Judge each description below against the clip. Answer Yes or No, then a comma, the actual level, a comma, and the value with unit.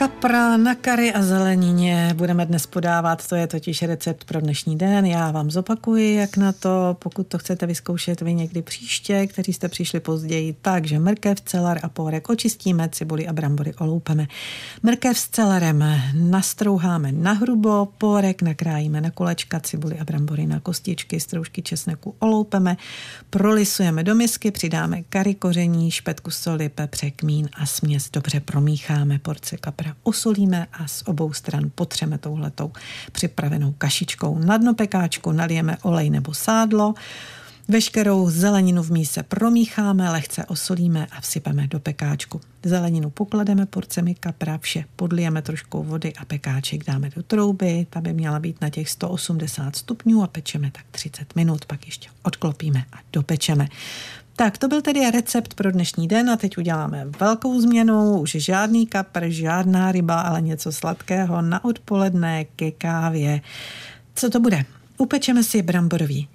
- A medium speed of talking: Yes, average, 150 wpm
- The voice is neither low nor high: Yes, medium, 170 Hz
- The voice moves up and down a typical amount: Yes, average, 4.0 semitones